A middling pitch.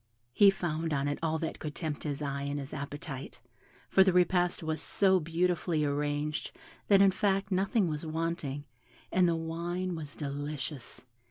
Yes: medium, 160 Hz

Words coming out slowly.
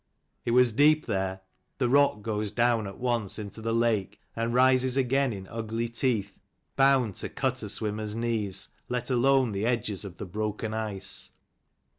No: average, 165 wpm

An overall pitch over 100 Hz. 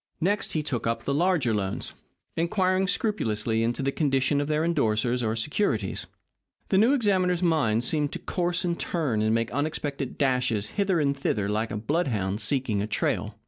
Yes: medium, 140 Hz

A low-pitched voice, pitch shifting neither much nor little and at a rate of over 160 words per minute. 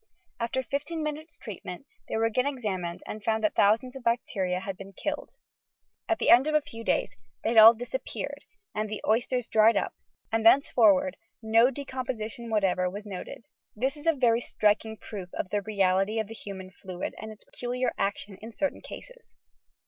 No: high, 225 Hz; average, 3.8 semitones; average, 190 wpm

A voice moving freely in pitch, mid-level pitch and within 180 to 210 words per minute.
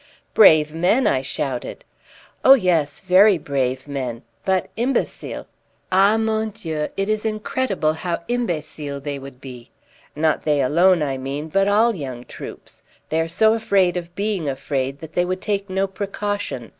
No: wide, 6.2 semitones; medium, 170 Hz; average, 155 wpm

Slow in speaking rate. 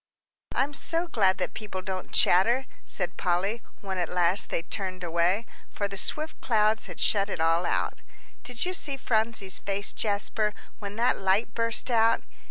No: average, 170 wpm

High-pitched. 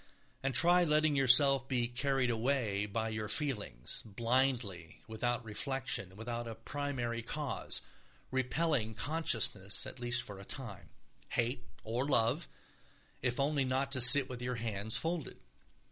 No: low, 125 Hz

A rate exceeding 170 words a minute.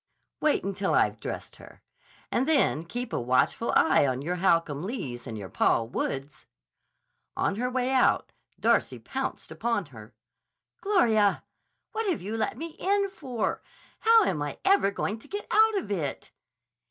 No: average, 160 wpm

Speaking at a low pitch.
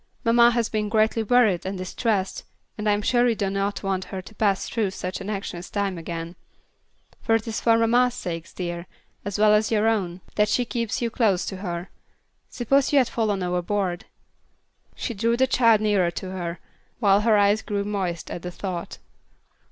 No: high, 205 Hz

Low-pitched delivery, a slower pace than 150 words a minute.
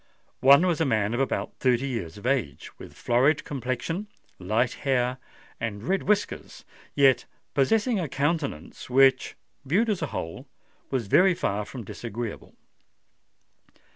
Yes: low, 130 Hz; slow, 135 wpm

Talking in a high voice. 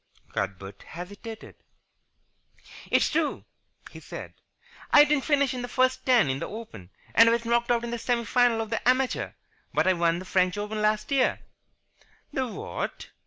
Yes: high, 230 Hz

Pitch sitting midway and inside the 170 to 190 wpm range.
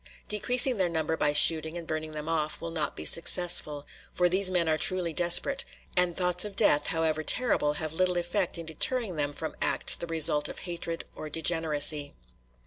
Yes: medium, 165 Hz; average, 185 wpm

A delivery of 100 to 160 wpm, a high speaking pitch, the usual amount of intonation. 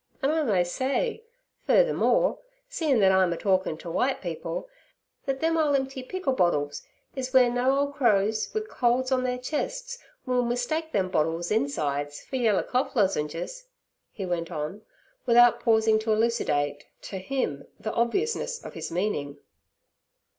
No: average, 145 wpm; high, 240 Hz; wide, 6.9 semitones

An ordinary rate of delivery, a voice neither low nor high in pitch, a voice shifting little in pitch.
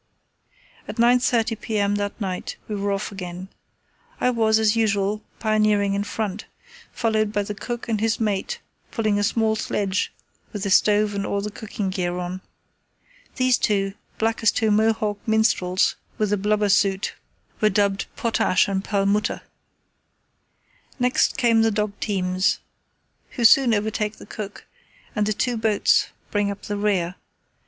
No: average, 150 wpm; high, 210 Hz; narrow, 1.7 semitones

